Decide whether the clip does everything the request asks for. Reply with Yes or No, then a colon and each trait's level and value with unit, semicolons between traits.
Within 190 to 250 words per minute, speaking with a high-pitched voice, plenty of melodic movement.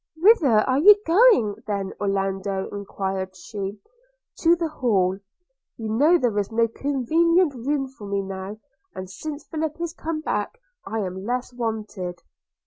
No: average, 150 wpm; high, 225 Hz; wide, 7.9 semitones